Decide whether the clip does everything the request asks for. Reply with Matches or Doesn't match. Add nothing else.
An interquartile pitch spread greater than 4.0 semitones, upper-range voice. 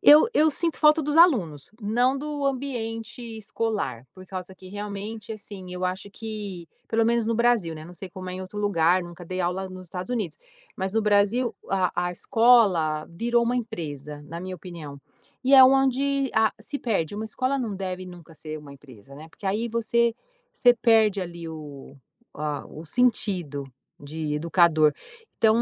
Matches